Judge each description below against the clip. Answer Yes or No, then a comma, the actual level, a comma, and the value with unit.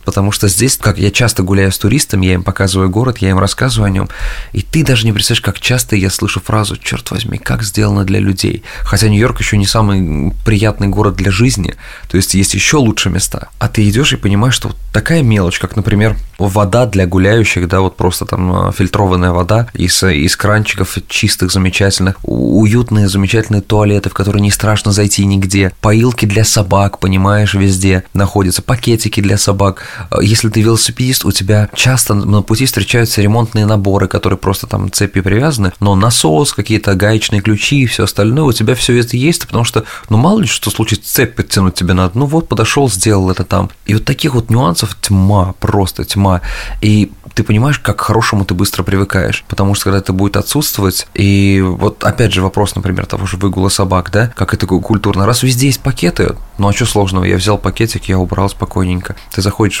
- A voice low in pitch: Yes, low, 100 Hz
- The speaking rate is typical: No, fast, 190 wpm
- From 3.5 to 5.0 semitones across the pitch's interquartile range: No, narrow, 2.5 semitones